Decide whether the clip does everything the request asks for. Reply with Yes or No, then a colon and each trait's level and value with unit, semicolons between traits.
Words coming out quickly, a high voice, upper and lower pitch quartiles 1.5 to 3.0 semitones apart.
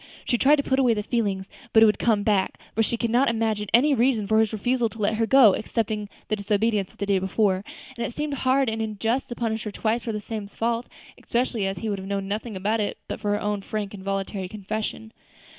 Yes: fast, 245 wpm; high, 220 Hz; narrow, 2.4 semitones